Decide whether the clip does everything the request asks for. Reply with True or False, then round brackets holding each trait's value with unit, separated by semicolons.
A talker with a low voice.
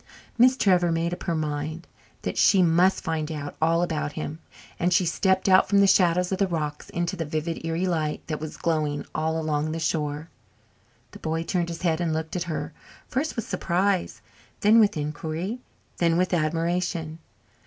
False (165 Hz)